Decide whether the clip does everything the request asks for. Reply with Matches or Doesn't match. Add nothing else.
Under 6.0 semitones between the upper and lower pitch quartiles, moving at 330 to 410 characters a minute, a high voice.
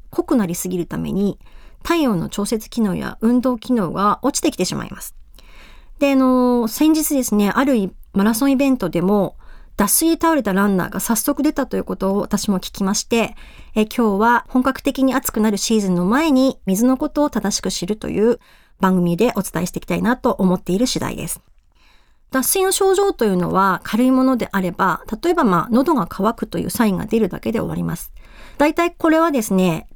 Matches